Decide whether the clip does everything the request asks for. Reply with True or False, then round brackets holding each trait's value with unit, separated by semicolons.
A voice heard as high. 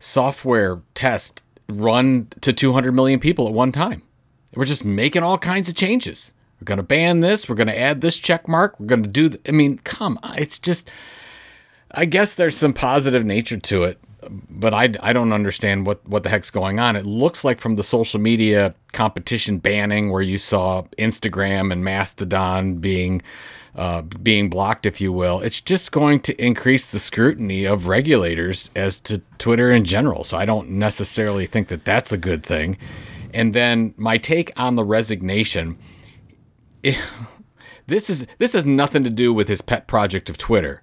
False (110 Hz)